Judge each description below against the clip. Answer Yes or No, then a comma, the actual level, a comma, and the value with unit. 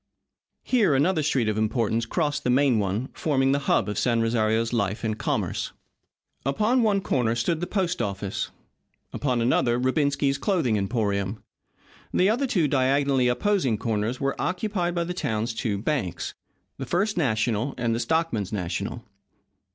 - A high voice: No, low, 125 Hz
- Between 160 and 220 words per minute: No, average, 150 wpm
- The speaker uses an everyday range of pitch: No, wide, 6.3 semitones